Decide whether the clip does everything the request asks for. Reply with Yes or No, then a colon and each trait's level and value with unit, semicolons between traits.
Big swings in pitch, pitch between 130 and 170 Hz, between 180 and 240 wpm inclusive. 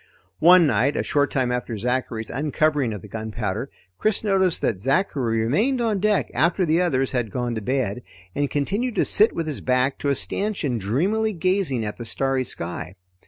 Yes: wide, 7.5 semitones; low, 135 Hz; average, 185 wpm